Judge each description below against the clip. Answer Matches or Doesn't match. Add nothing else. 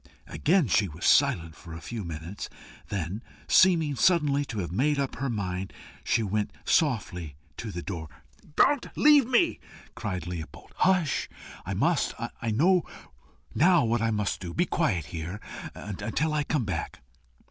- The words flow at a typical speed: Matches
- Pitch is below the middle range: Matches